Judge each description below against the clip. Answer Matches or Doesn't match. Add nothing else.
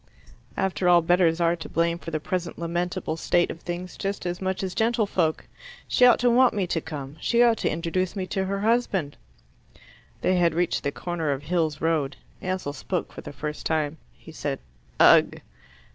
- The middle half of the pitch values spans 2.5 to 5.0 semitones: Matches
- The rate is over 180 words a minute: Matches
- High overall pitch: Doesn't match